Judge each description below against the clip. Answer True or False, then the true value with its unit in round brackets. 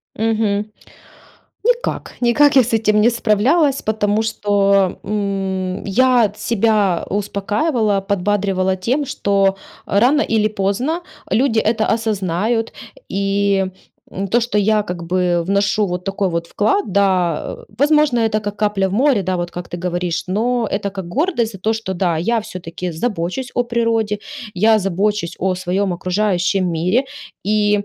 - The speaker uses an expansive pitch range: False (3.1 semitones)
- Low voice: False (205 Hz)